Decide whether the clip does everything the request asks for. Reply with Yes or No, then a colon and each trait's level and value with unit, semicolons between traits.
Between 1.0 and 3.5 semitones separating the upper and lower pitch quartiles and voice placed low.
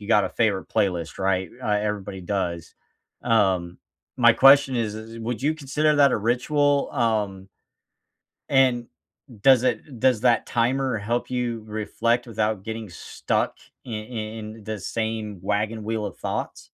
Yes: average, 2.9 semitones; low, 110 Hz